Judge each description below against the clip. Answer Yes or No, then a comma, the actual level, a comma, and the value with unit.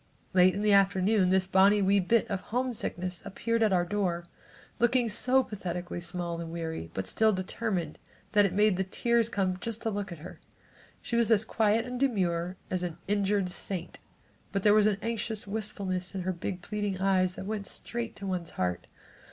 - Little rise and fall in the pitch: No, average, 3.1 semitones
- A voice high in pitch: Yes, high, 195 Hz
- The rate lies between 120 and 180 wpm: No, average, 190 wpm